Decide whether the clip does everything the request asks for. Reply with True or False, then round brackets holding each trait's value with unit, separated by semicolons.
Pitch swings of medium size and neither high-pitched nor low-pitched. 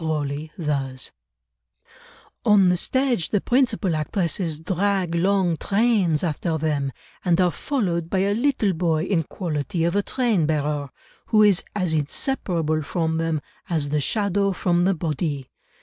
True (4.2 semitones; 170 Hz)